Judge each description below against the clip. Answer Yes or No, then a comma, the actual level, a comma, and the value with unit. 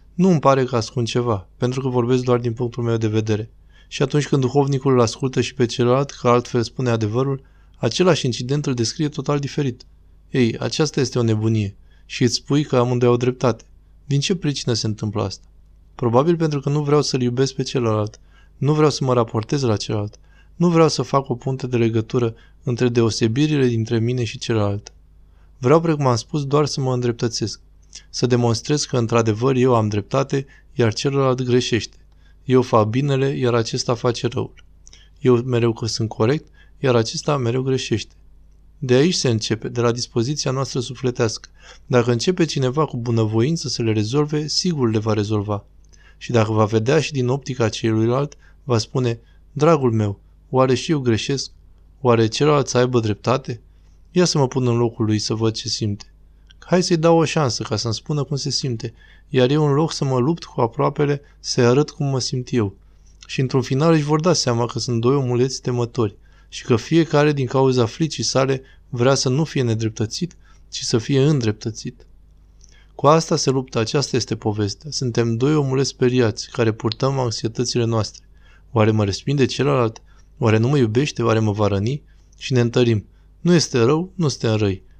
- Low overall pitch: Yes, low, 120 Hz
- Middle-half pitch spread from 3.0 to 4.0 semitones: Yes, average, 3.7 semitones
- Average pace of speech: No, fast, 185 wpm